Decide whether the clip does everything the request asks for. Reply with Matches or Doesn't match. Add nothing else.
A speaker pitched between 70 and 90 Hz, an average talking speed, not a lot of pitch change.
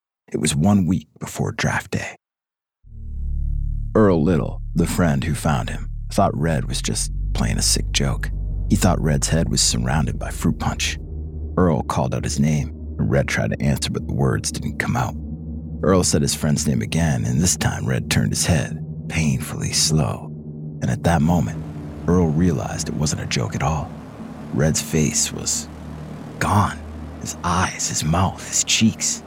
Matches